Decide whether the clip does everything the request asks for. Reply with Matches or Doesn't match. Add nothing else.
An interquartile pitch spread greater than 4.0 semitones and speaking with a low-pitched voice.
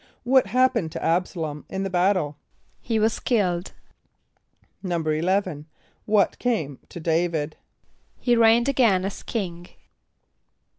Doesn't match